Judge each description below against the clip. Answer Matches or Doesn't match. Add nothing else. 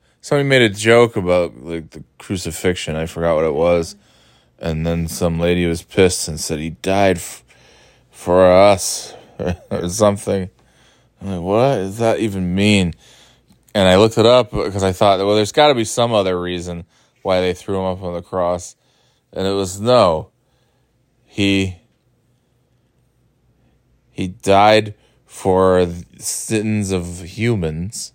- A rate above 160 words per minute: Doesn't match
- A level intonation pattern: Doesn't match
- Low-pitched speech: Matches